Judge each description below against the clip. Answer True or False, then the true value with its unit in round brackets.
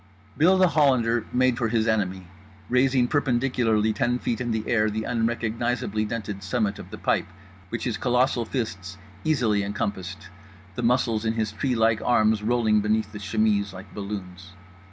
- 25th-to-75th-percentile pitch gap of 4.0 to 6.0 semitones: False (2.7 semitones)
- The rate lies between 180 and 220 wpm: False (155 wpm)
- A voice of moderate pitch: False (110 Hz)